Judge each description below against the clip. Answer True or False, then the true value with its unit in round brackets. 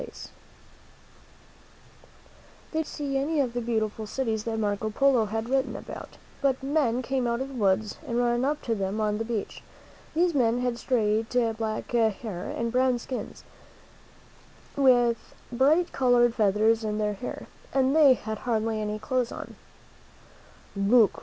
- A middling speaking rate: True (155 wpm)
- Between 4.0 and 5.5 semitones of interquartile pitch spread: False (3.2 semitones)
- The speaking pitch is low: False (235 Hz)